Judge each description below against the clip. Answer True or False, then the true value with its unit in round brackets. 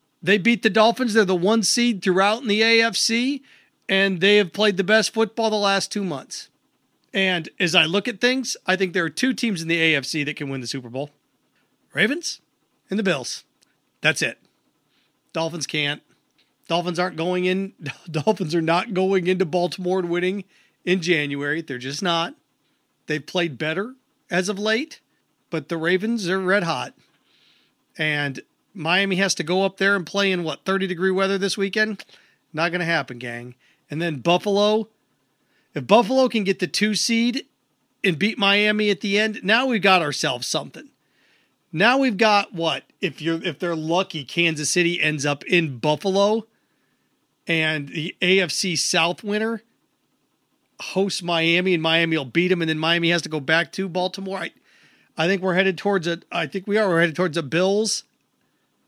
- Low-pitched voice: False (185 Hz)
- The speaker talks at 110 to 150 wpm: False (175 wpm)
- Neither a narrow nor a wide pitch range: True (4.0 semitones)